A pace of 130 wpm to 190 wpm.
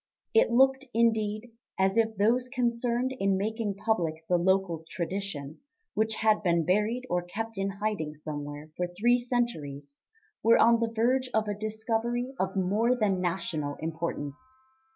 Yes: average, 150 wpm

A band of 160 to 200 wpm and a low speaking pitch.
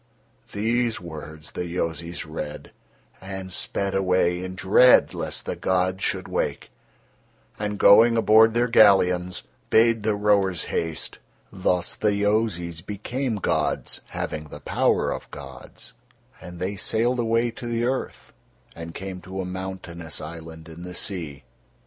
No: slow, 135 wpm; very low, 95 Hz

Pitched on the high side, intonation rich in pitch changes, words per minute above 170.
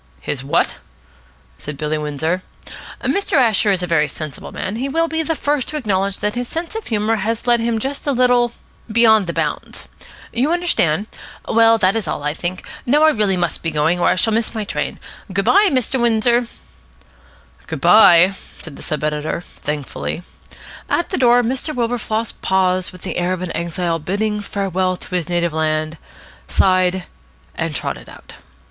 Yes: high, 200 Hz; wide, 5.8 semitones; average, 180 wpm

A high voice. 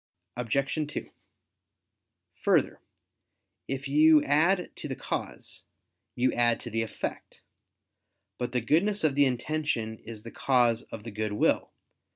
No: low, 130 Hz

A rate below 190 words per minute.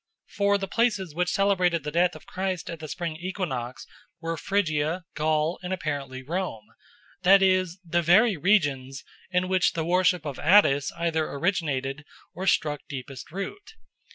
Yes: average, 155 wpm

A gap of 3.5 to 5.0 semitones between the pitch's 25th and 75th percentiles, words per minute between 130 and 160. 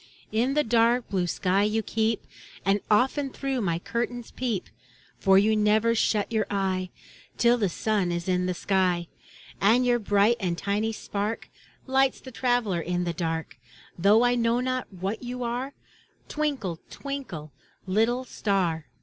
Yes: average, 4.5 semitones; average, 155 wpm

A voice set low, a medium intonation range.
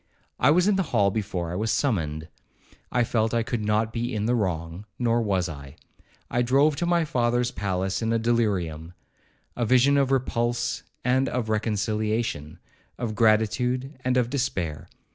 Yes: low, 115 Hz; average, 4.1 semitones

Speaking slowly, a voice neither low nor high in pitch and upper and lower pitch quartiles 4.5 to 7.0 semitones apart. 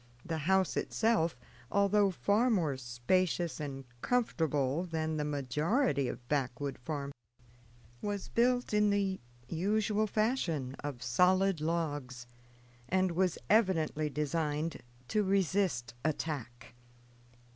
Yes: slow, 105 wpm; medium, 165 Hz; wide, 5.6 semitones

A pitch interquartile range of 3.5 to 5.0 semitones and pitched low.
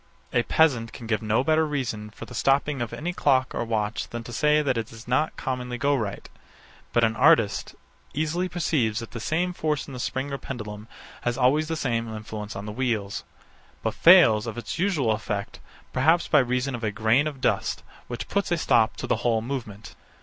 Yes: average, 4.7 semitones; low, 125 Hz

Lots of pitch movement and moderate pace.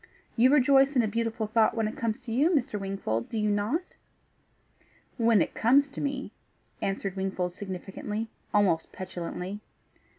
No: average, 4.4 semitones; average, 155 wpm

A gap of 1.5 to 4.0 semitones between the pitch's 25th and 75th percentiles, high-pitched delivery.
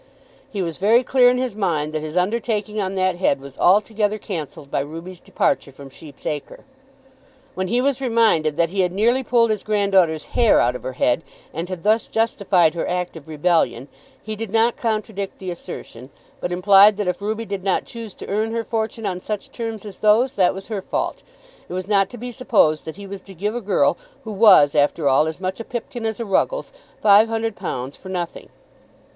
No: average, 4.6 semitones; high, 195 Hz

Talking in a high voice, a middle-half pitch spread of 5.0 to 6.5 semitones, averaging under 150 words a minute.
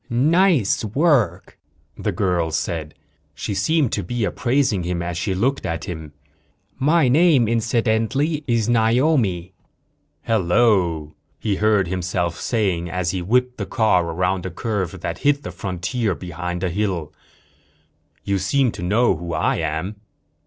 No: low, 100 Hz; wide, 5.6 semitones; average, 140 wpm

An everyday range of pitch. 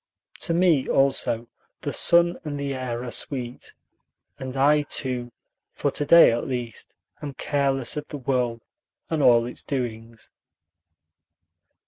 Yes: average, 3.2 semitones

